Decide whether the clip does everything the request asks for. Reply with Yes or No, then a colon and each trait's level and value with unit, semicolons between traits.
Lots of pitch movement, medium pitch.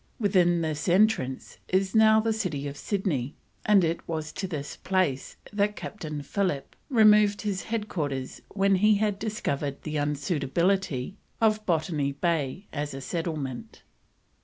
Yes: wide, 6.0 semitones; medium, 175 Hz